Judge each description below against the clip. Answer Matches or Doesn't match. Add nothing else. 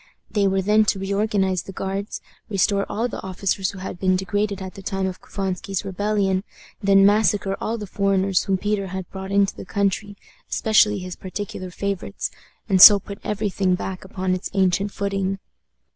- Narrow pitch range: Matches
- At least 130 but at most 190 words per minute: Matches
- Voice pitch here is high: Matches